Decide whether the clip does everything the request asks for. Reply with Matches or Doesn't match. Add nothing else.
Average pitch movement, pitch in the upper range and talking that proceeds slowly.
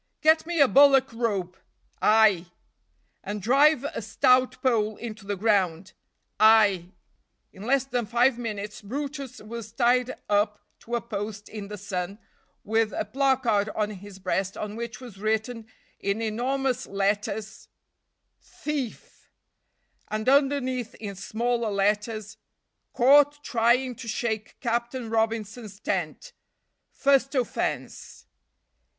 Matches